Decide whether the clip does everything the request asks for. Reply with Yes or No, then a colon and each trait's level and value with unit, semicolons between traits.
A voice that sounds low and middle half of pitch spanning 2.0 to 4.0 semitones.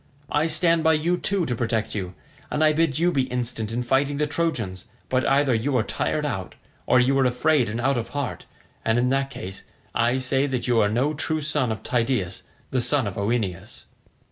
No: low, 130 Hz; average, 4.4 semitones